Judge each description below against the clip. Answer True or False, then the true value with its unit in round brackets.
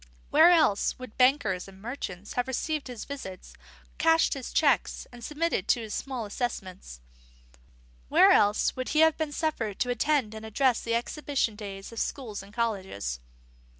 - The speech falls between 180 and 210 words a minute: False (160 wpm)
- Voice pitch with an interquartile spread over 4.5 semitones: True (5.5 semitones)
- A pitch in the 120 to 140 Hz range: False (240 Hz)